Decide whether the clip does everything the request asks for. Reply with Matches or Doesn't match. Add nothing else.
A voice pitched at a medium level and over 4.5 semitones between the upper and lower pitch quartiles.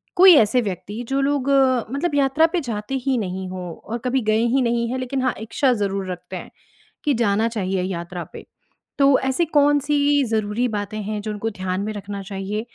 Doesn't match